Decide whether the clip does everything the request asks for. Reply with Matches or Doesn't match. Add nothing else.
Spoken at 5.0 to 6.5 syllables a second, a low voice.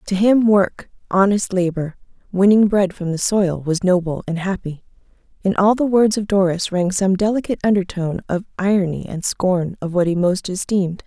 Doesn't match